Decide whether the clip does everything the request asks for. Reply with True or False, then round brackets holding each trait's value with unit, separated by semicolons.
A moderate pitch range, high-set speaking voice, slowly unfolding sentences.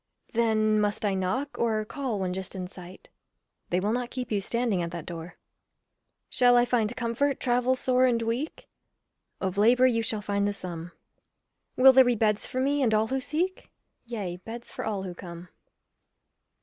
False (4.5 semitones; 220 Hz; 180 wpm)